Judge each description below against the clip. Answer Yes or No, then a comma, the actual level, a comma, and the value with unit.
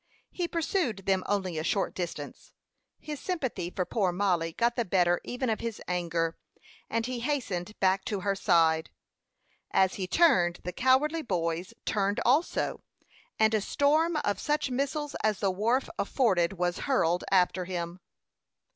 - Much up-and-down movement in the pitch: Yes, wide, 6.4 semitones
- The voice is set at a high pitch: Yes, high, 195 Hz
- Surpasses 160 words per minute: No, average, 155 wpm